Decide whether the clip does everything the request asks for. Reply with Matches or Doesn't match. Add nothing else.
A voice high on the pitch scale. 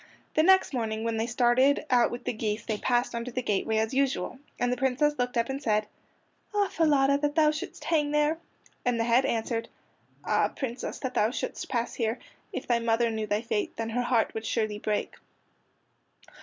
Matches